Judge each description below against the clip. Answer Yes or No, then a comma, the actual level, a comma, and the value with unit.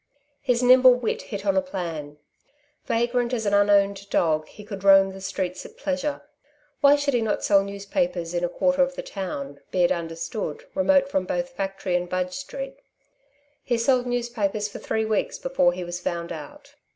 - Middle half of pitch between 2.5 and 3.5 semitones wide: No, wide, 5.6 semitones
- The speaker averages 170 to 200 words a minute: Yes, average, 185 wpm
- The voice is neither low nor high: No, high, 200 Hz